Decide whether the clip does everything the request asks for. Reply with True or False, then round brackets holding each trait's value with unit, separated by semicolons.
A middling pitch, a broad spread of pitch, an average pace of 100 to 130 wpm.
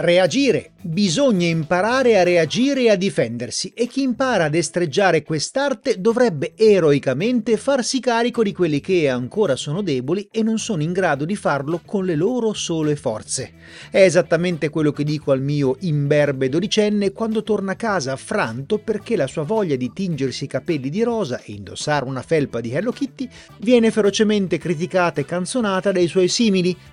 False (180 Hz; 6.7 semitones; 165 wpm)